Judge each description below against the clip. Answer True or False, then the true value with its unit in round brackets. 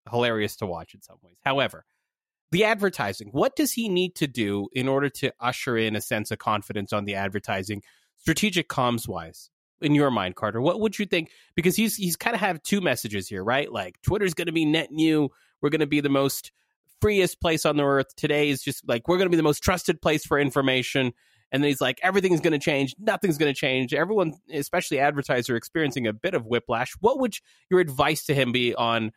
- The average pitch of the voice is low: False (145 Hz)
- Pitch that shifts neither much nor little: False (6.6 semitones)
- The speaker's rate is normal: False (210 wpm)